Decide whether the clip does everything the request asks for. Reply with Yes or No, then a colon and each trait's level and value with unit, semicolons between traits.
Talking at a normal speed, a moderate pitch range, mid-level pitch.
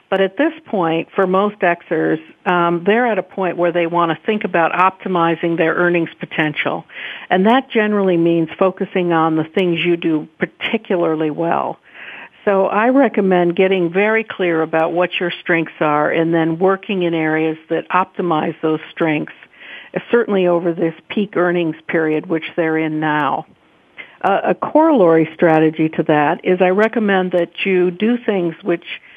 Yes: average, 160 wpm; average, 3.0 semitones; medium, 175 Hz